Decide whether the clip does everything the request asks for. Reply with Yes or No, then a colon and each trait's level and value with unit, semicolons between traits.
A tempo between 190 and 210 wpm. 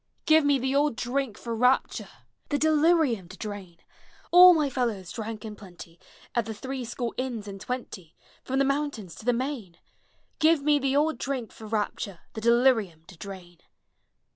No: average, 170 wpm